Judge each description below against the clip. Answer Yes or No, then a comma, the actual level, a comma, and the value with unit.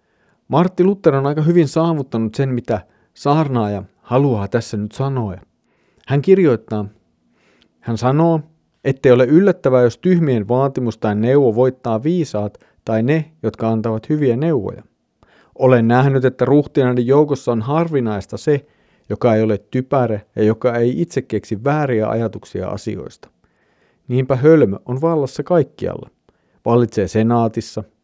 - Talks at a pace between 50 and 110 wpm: No, average, 130 wpm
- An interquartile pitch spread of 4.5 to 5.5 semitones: Yes, average, 4.8 semitones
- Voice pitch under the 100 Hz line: No, low, 125 Hz